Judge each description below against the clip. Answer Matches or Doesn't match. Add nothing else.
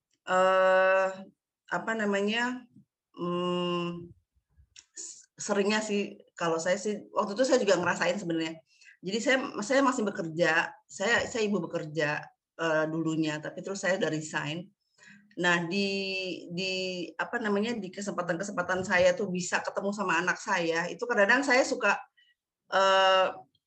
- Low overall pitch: Doesn't match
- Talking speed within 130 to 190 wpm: Matches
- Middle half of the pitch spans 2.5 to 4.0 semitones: Matches